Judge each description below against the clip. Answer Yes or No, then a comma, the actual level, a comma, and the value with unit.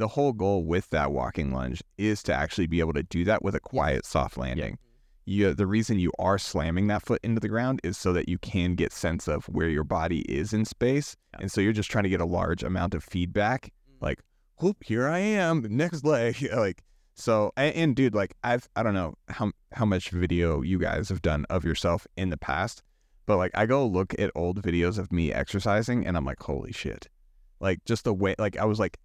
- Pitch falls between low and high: No, very low, 95 Hz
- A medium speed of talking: No, fast, 230 wpm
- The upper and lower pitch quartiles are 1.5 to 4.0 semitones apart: No, average, 4.4 semitones